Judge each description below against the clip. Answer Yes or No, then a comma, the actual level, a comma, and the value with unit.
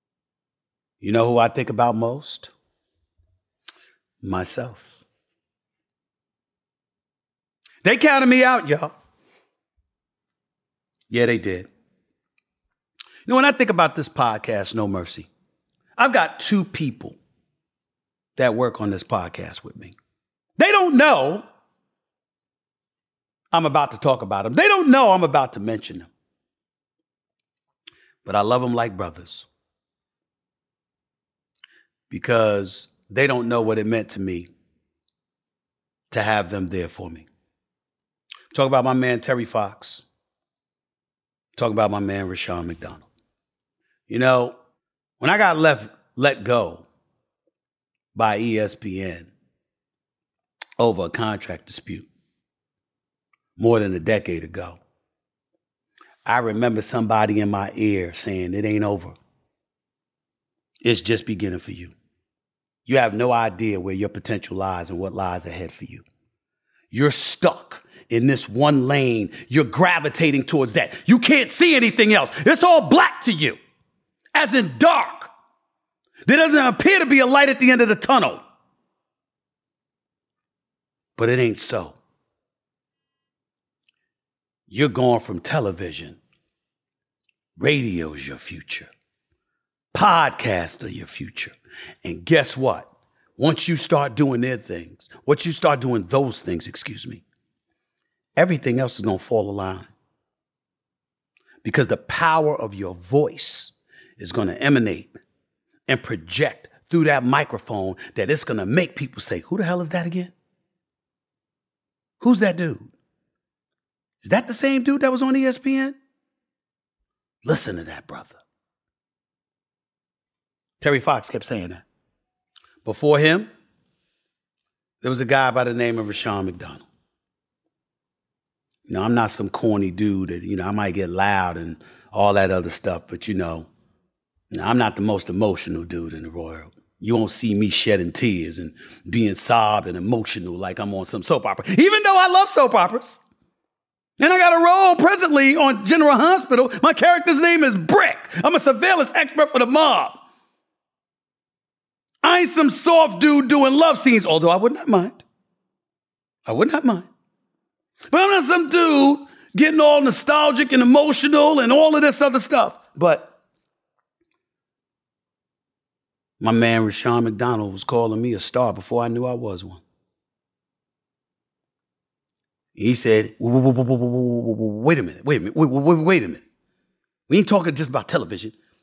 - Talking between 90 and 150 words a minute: Yes, average, 140 wpm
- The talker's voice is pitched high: No, low, 125 Hz